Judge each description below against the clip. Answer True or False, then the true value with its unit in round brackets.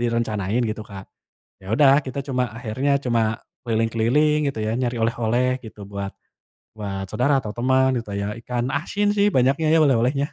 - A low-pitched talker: True (120 Hz)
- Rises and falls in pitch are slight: False (3.1 semitones)